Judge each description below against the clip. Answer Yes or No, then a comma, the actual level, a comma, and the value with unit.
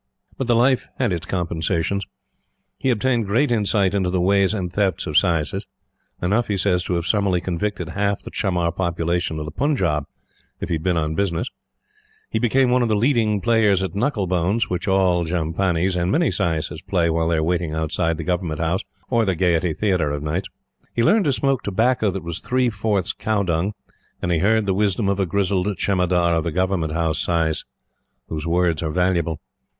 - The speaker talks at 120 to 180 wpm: No, average, 195 wpm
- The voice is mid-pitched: No, very low, 95 Hz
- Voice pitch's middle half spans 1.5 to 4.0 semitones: Yes, average, 3.6 semitones